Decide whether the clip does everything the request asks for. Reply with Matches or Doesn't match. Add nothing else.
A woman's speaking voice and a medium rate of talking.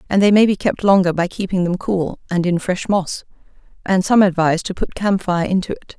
Doesn't match